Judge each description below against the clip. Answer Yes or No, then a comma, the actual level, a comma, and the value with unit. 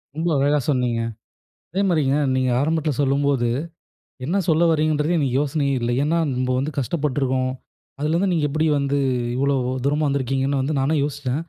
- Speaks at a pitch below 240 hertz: Yes, medium, 140 Hz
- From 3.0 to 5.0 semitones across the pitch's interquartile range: No, narrow, 2.6 semitones